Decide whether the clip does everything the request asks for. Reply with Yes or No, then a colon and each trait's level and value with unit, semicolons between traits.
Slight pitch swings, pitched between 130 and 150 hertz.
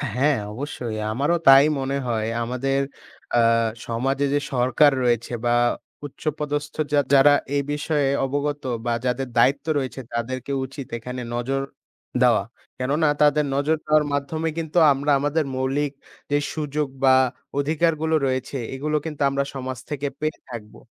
Yes: narrow, 2.3 semitones; medium, 140 Hz